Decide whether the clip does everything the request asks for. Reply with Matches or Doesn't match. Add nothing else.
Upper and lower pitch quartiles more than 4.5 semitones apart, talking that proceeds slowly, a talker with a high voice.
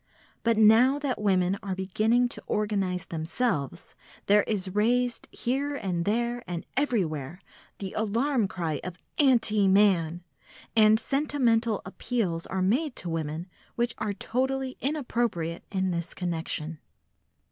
Matches